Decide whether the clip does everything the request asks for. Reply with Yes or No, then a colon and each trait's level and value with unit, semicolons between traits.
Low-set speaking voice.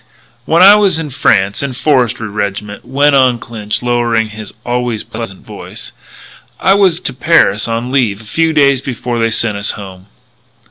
Yes: low, 120 Hz